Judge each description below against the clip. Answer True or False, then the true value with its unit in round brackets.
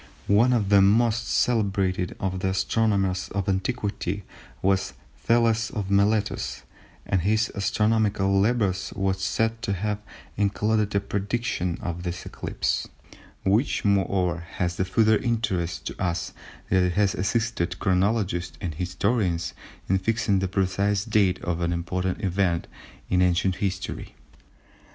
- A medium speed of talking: False (130 wpm)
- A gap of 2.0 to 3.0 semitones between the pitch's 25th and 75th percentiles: True (2.6 semitones)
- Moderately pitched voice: False (100 Hz)